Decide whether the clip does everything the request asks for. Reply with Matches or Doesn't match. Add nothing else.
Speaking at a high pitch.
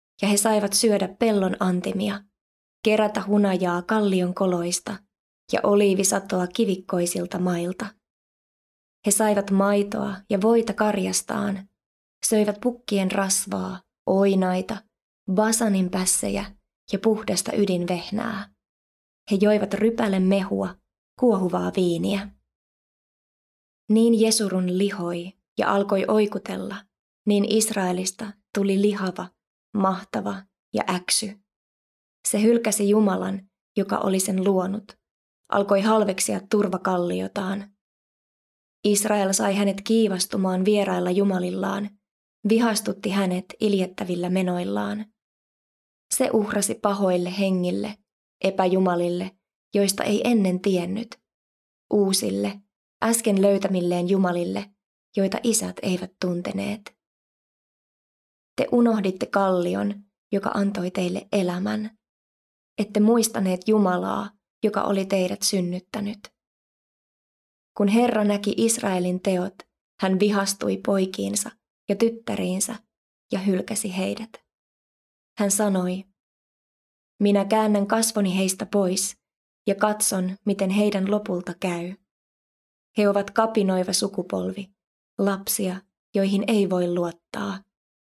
Matches